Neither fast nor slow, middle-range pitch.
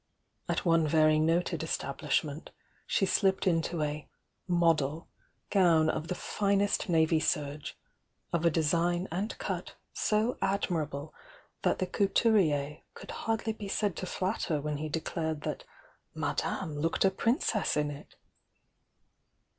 No: slow, 130 wpm; medium, 165 Hz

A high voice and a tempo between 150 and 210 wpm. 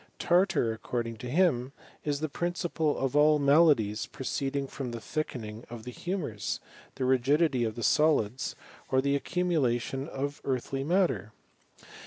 No: low, 135 Hz; average, 155 wpm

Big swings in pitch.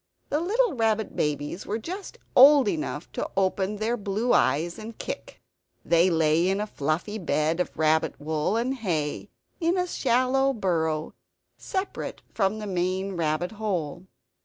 Yes: wide, 6.3 semitones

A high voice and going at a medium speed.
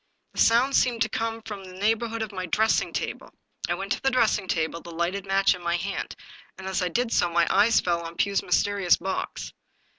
No: high, 195 Hz; fast, 215 wpm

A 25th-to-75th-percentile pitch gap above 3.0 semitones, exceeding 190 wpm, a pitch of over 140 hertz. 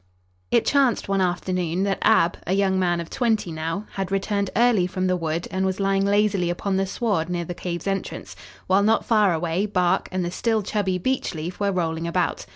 No: narrow, 2.5 semitones; average, 200 wpm; high, 190 Hz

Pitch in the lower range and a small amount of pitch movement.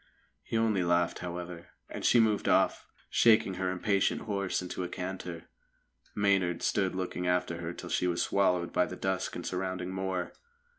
Yes: very low, 90 Hz; narrow, 1.6 semitones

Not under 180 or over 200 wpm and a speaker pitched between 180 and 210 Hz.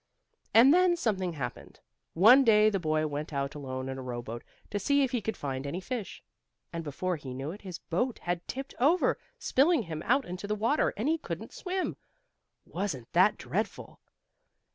Yes: average, 185 wpm; medium, 185 Hz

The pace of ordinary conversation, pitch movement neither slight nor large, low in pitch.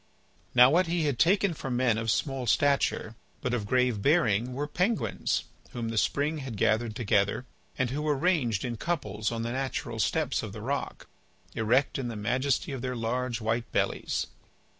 Yes: average, 180 wpm; average, 4.0 semitones; low, 125 Hz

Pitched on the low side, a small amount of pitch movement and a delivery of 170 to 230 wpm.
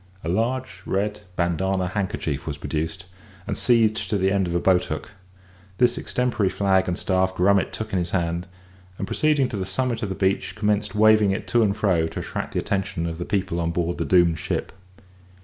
No: very low, 95 Hz; average, 3.3 semitones; average, 200 wpm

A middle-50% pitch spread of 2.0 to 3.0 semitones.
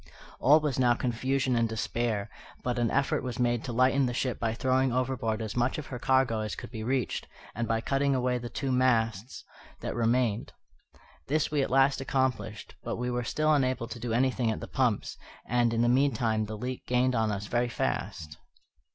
Yes: narrow, 2.5 semitones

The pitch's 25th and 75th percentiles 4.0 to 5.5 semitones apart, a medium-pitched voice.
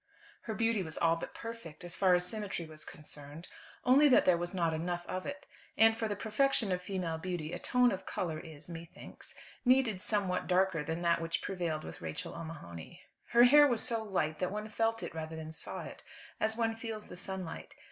Yes: average, 5.2 semitones; medium, 180 Hz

